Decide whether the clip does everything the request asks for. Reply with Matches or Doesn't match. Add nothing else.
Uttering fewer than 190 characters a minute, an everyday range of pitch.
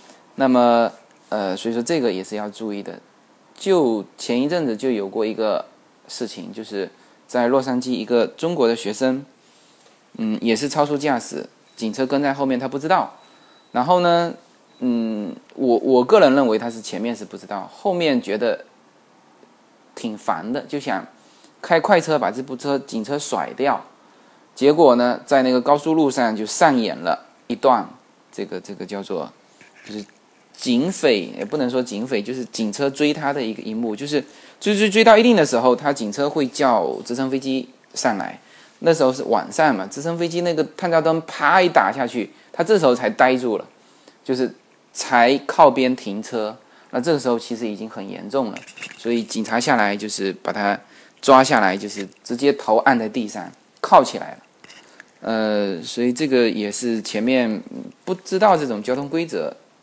Doesn't match